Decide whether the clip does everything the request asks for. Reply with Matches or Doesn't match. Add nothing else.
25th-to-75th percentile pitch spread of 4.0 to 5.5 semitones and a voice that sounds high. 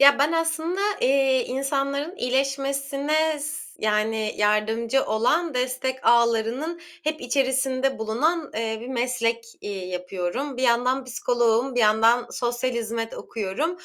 Doesn't match